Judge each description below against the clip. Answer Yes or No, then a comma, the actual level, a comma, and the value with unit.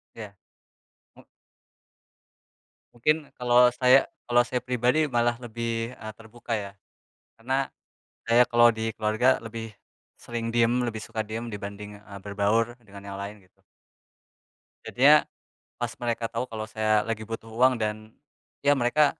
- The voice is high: No, low, 115 Hz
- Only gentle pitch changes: Yes, narrow, 2.1 semitones